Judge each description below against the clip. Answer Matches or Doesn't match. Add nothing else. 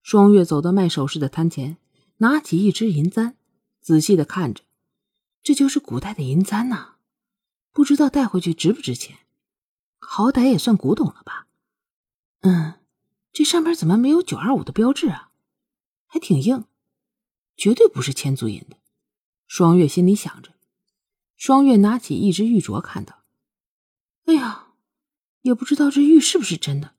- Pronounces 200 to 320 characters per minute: Matches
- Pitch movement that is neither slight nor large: Doesn't match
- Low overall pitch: Doesn't match